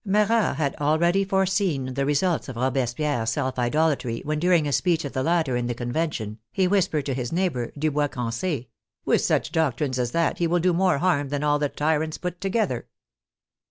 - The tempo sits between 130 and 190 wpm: No, fast, 205 wpm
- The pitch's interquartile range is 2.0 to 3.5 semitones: No, average, 5.2 semitones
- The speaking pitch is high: No, medium, 150 Hz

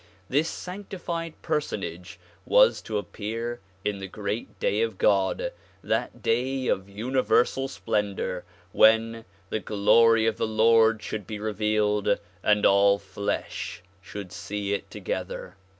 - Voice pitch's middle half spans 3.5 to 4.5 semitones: No, narrow, 2.4 semitones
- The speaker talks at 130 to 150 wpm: Yes, slow, 135 wpm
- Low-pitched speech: Yes, low, 110 Hz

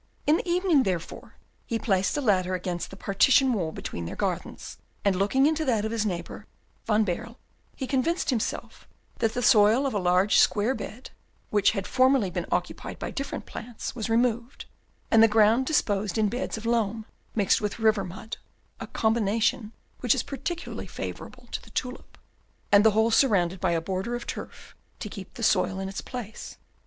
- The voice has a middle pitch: No, high, 220 Hz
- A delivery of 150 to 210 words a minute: Yes, average, 185 wpm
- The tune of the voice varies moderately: Yes, average, 4.0 semitones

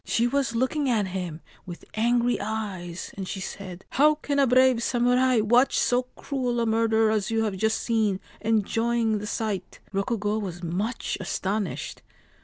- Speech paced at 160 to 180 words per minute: Yes, average, 170 wpm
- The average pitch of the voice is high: Yes, high, 220 Hz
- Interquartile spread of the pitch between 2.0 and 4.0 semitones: Yes, average, 3.5 semitones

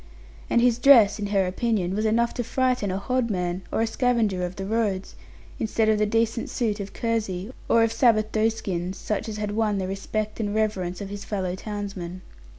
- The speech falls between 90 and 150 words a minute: No, average, 195 wpm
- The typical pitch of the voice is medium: No, high, 210 Hz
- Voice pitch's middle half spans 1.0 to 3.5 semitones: Yes, average, 2.7 semitones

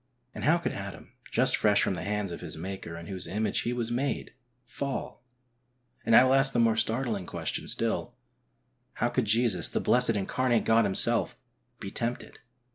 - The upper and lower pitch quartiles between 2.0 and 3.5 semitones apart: No, average, 3.9 semitones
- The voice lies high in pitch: No, low, 115 Hz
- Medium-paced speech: Yes, average, 180 wpm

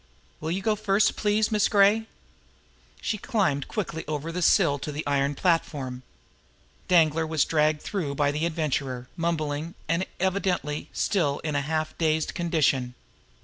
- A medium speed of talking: Yes, average, 145 wpm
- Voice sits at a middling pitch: Yes, medium, 160 Hz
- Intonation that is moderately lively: Yes, average, 4.4 semitones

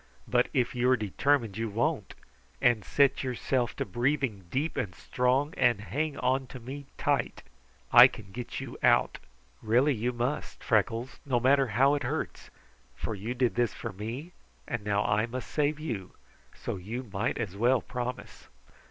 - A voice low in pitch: Yes, low, 120 Hz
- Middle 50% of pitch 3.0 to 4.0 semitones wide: Yes, average, 3.4 semitones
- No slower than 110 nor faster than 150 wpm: No, average, 170 wpm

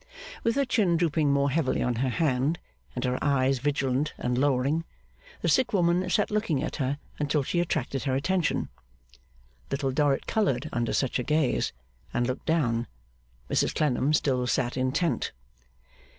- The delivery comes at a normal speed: Yes, average, 155 wpm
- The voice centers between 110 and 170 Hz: Yes, medium, 140 Hz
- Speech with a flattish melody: No, average, 4.3 semitones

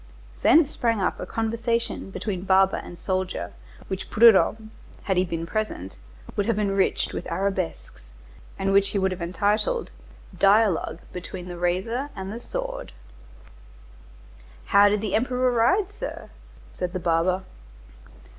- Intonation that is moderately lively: Yes, average, 3.7 semitones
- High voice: Yes, high, 195 Hz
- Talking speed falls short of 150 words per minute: Yes, slow, 135 wpm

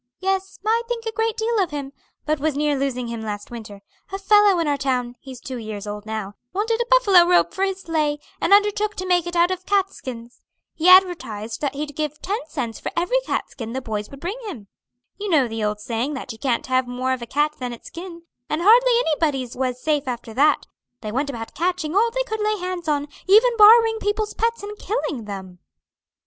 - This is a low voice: No, very high, 305 Hz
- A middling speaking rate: No, fast, 220 wpm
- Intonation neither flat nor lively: No, wide, 8.2 semitones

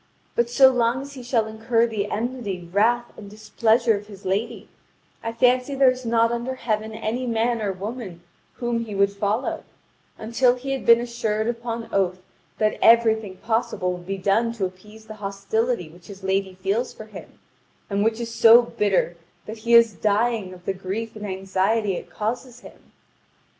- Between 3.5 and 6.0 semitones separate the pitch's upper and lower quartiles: No, average, 3.0 semitones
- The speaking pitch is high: Yes, high, 220 Hz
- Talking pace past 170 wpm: Yes, average, 180 wpm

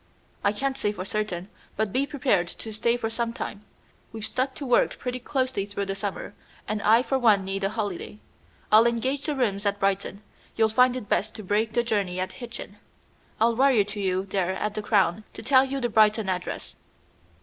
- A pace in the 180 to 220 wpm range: Yes, fast, 205 wpm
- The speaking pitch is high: Yes, high, 215 Hz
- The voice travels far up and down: No, average, 3.4 semitones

